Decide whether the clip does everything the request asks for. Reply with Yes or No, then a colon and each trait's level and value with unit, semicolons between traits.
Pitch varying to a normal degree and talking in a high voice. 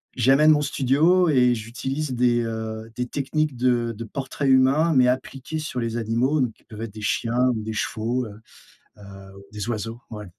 No: average, 3.1 semitones; low, 125 Hz